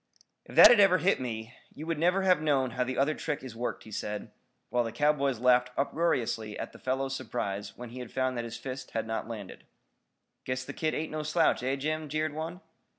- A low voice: Yes, low, 130 Hz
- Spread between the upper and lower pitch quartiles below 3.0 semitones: No, average, 4.4 semitones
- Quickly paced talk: Yes, fast, 215 wpm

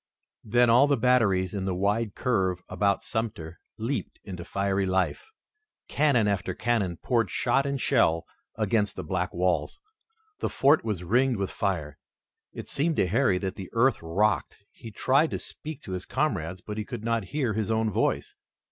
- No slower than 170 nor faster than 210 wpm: Yes, average, 175 wpm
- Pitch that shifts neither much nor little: Yes, average, 4.6 semitones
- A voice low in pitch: Yes, low, 105 Hz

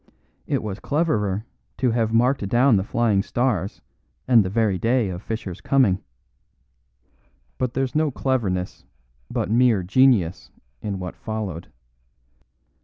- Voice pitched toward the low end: Yes, low, 110 Hz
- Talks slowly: Yes, slow, 125 wpm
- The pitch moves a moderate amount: Yes, average, 4.7 semitones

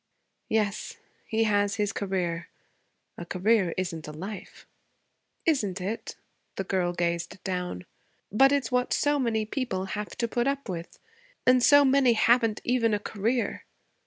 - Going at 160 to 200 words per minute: No, average, 145 wpm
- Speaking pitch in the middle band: No, high, 210 Hz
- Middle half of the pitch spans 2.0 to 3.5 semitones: No, average, 4.8 semitones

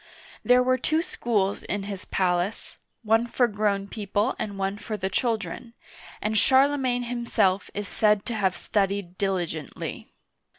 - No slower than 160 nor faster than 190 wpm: No, average, 145 wpm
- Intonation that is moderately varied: Yes, average, 3.4 semitones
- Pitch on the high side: Yes, high, 205 Hz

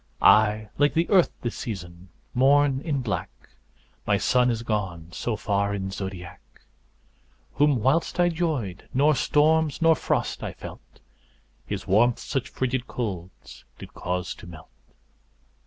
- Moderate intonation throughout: No, wide, 7.1 semitones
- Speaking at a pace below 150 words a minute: Yes, average, 140 wpm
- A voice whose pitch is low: Yes, low, 120 Hz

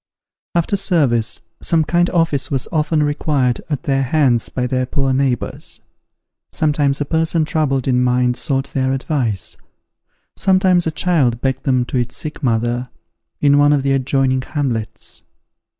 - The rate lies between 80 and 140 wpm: No, average, 150 wpm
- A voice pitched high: No, low, 135 Hz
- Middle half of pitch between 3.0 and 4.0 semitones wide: Yes, average, 3.5 semitones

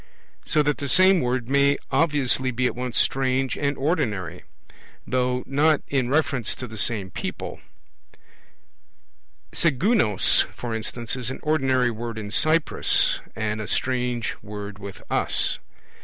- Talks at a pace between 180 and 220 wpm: No, slow, 135 wpm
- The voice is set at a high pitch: No, low, 125 Hz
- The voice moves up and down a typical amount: Yes, average, 3.6 semitones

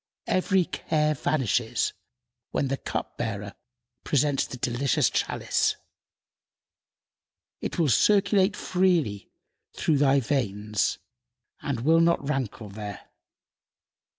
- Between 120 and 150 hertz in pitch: Yes, medium, 140 Hz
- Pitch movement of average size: No, wide, 6.3 semitones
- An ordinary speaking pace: No, slow, 95 wpm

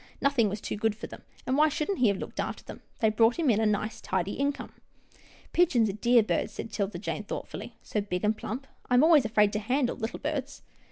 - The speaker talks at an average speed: No, fast, 240 wpm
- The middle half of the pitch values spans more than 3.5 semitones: Yes, average, 4.9 semitones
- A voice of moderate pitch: No, high, 225 Hz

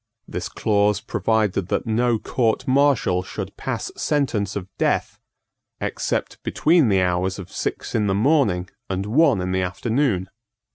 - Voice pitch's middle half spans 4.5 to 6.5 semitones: Yes, average, 4.8 semitones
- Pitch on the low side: Yes, low, 105 Hz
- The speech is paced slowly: No, average, 145 wpm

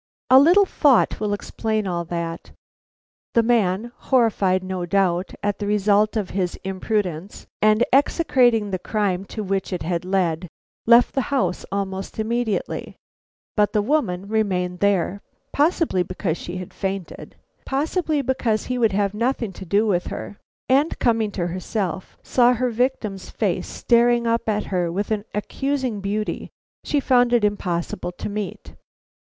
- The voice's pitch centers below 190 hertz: No, high, 210 Hz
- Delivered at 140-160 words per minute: Yes, average, 150 wpm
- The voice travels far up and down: No, average, 4.3 semitones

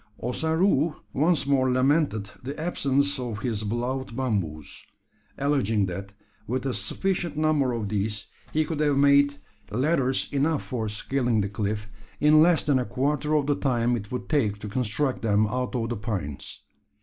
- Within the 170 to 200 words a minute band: No, average, 160 wpm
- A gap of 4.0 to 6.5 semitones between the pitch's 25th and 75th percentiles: Yes, average, 5.1 semitones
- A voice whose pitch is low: Yes, low, 130 Hz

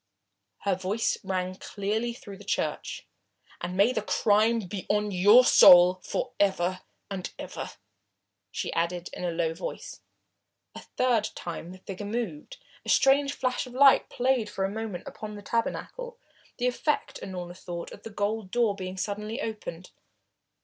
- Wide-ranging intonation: No, average, 3.8 semitones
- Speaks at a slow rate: No, average, 155 wpm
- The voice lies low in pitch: No, high, 205 Hz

